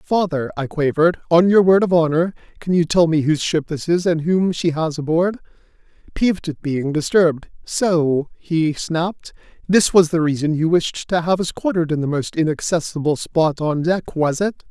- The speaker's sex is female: No, male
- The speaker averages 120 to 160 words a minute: No, average, 190 wpm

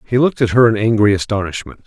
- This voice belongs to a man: Yes, male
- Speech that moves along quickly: Yes, fast, 225 wpm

